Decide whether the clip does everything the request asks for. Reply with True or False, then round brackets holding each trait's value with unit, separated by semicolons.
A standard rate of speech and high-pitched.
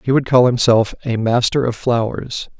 False (185 wpm; 120 Hz)